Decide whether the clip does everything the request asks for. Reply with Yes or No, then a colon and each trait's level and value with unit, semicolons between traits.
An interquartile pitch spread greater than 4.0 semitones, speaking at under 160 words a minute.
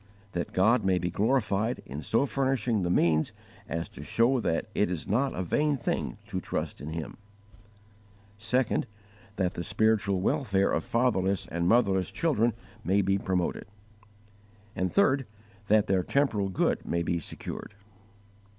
Yes: average, 4.9 semitones; average, 145 wpm